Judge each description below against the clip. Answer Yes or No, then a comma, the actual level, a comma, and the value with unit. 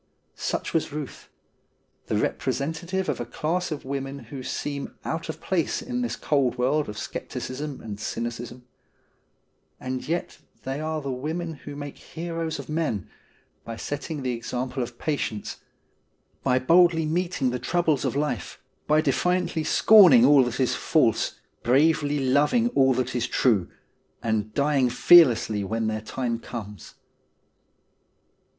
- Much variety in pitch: No, average, 4.5 semitones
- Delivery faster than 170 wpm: No, average, 140 wpm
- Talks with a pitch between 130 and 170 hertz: Yes, medium, 140 Hz